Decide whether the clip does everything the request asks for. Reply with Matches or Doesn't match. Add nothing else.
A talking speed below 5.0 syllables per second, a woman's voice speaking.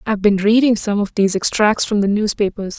Doesn't match